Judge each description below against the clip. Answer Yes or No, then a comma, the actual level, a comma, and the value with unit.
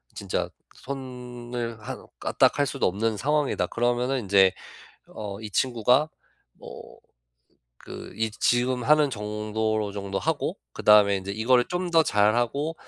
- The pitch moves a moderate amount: Yes, average, 3.5 semitones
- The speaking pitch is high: No, low, 120 Hz